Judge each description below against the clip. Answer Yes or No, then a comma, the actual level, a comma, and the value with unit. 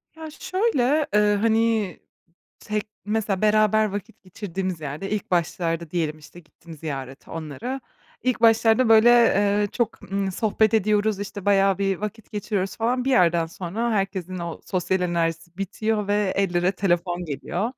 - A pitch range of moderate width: Yes, average, 3.9 semitones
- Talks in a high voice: Yes, high, 200 Hz